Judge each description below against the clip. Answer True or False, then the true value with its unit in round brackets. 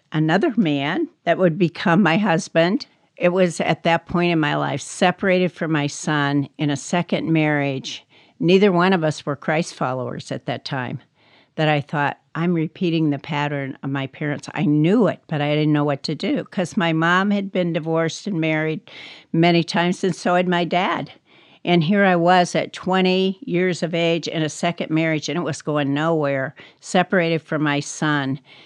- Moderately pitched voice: True (165 Hz)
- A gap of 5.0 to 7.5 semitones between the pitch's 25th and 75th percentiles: False (3.3 semitones)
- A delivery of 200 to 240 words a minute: False (190 wpm)